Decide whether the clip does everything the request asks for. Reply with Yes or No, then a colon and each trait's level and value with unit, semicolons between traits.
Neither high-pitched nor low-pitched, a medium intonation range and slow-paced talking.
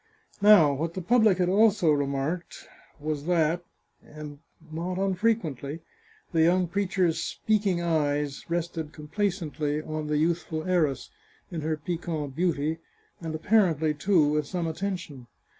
Yes: medium, 165 Hz; average, 3.2 semitones; slow, 125 wpm